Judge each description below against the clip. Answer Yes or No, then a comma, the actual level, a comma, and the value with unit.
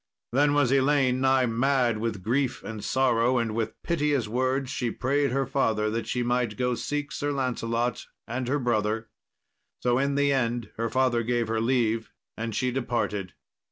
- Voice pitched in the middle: No, low, 125 Hz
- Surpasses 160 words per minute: Yes, average, 170 wpm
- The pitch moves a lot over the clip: No, average, 2.7 semitones